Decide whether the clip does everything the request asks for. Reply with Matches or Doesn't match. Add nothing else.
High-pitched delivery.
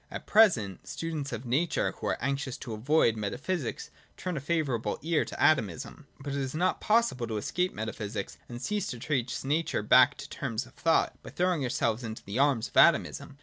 Doesn't match